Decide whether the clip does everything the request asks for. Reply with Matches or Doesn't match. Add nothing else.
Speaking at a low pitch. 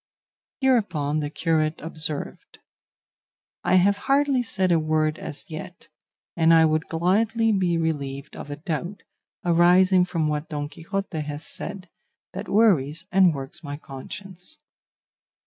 Doesn't match